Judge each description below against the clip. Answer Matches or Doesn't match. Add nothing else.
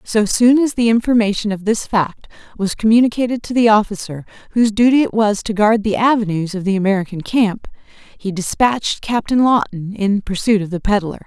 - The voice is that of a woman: Matches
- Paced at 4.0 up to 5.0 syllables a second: Doesn't match